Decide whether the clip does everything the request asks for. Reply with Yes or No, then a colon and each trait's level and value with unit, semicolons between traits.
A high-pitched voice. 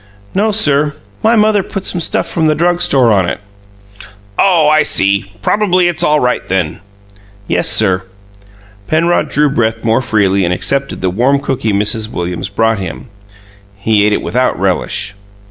No: low, 125 Hz